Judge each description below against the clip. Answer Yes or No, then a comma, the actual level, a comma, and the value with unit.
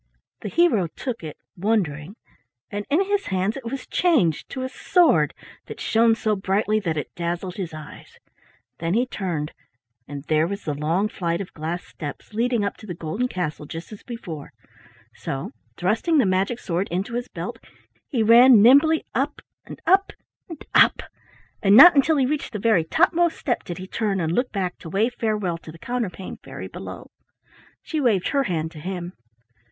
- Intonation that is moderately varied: No, wide, 6.4 semitones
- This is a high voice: Yes, high, 200 Hz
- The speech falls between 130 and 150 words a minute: No, average, 180 wpm